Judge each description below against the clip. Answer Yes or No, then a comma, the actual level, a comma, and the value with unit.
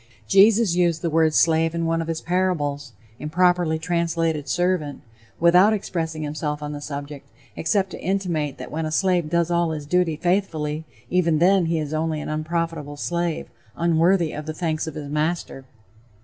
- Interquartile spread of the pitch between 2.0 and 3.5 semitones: Yes, narrow, 2.4 semitones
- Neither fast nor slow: Yes, average, 170 wpm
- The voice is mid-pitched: Yes, medium, 165 Hz